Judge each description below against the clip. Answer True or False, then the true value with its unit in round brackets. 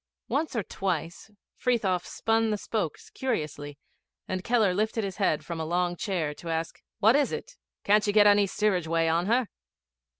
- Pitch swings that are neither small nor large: True (4.7 semitones)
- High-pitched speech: True (195 Hz)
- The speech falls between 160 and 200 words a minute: True (175 wpm)